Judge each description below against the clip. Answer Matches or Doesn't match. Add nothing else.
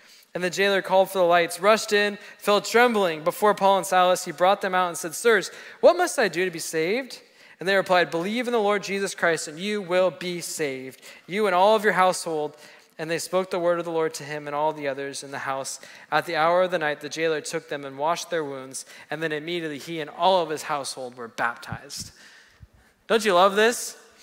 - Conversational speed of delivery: Doesn't match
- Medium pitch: Matches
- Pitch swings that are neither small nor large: Matches